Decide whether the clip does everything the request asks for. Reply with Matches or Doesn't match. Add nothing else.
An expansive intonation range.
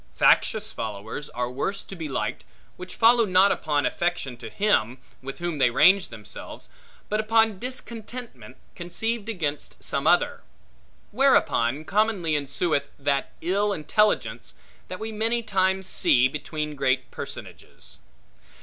Matches